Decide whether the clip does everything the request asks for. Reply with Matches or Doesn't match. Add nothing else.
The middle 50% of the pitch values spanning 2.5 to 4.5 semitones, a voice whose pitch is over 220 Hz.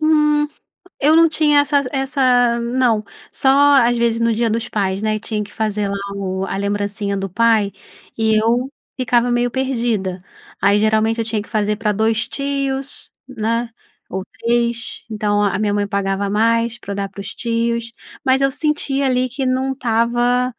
Matches